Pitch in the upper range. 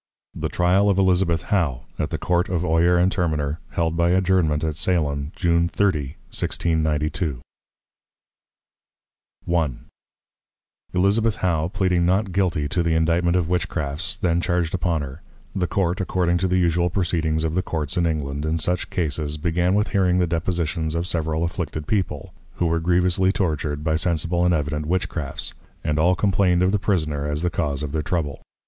No: very low, 85 Hz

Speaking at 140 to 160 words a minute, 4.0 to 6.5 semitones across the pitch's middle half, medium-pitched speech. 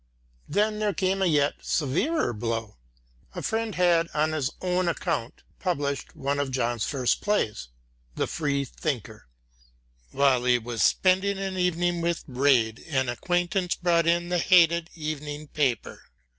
Yes: average, 145 wpm; average, 5.3 semitones; medium, 155 Hz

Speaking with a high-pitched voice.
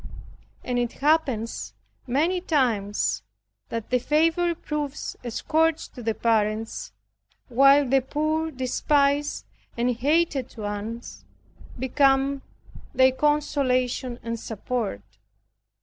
Yes: very high, 260 Hz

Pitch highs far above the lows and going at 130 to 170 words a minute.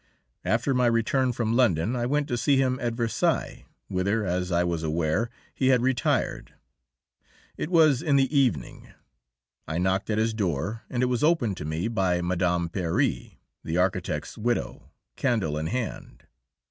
Yes: wide, 6.1 semitones; average, 160 wpm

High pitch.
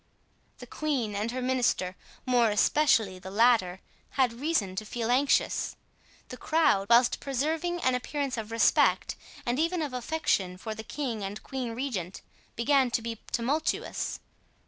Yes: high, 245 Hz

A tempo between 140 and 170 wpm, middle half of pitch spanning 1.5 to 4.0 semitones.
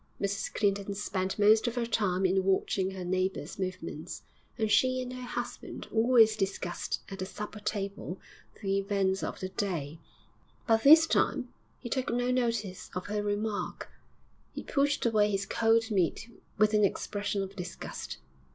Yes: average, 160 wpm; average, 3.0 semitones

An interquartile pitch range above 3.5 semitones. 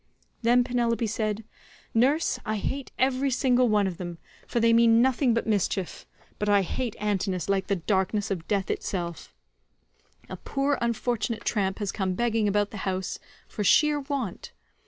Yes: average, 3.9 semitones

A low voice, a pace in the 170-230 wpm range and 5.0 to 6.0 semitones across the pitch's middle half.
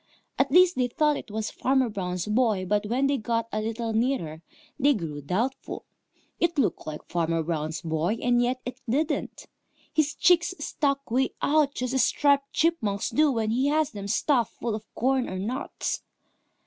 No: high, 240 Hz; average, 175 wpm; average, 5.3 semitones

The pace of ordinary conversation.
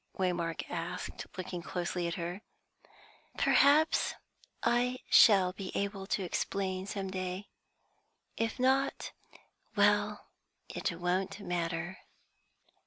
No: slow, 100 wpm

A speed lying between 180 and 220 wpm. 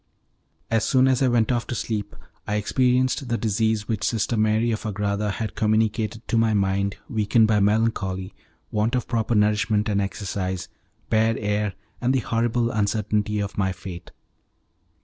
No: average, 160 wpm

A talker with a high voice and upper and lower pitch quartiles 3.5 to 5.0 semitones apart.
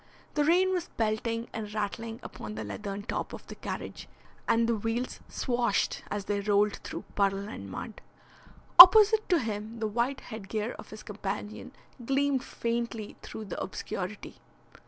No: high, 220 Hz; average, 3.0 semitones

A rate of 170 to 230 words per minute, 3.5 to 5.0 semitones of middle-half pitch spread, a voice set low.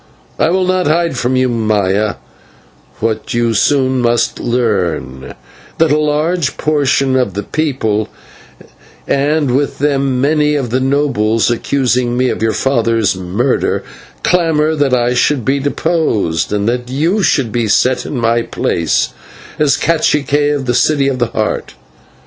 No: average, 150 wpm; average, 4.4 semitones; low, 130 Hz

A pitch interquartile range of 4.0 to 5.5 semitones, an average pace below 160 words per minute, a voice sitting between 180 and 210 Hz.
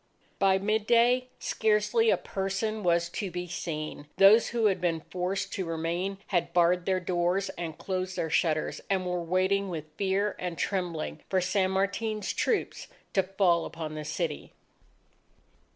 No: narrow, 2.6 semitones; average, 150 wpm; medium, 185 Hz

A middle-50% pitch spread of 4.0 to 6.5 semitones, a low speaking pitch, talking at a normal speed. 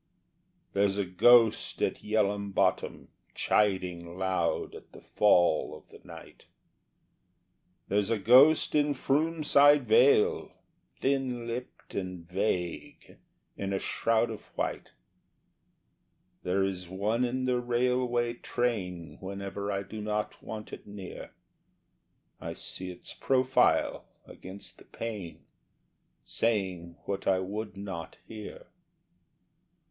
No: average, 4.4 semitones; low, 105 Hz; slow, 115 wpm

